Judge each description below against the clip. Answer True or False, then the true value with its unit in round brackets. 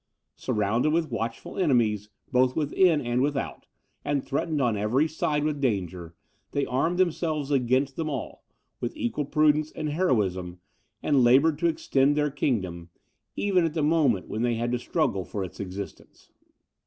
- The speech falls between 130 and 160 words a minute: True (155 wpm)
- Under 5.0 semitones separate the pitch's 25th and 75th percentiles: False (5.4 semitones)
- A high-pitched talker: False (135 Hz)